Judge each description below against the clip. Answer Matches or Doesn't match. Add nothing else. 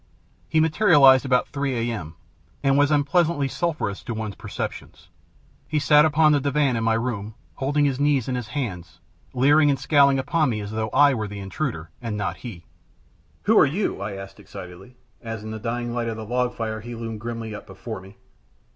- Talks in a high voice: Doesn't match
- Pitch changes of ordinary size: Matches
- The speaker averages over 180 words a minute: Matches